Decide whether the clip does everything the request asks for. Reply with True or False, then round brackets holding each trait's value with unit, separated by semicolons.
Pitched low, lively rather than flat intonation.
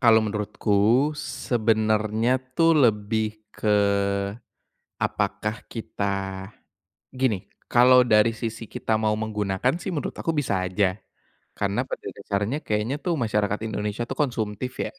False (110 Hz; 2.7 semitones)